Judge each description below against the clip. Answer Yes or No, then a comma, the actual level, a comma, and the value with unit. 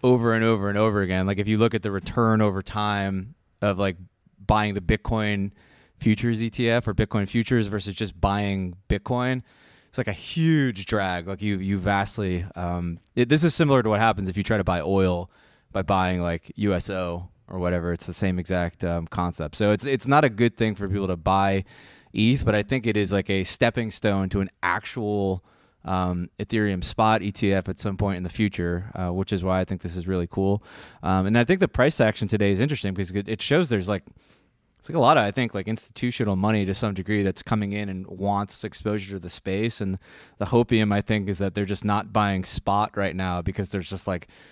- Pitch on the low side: Yes, low, 100 Hz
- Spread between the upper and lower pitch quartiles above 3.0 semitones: No, average, 2.7 semitones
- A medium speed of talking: No, fast, 220 wpm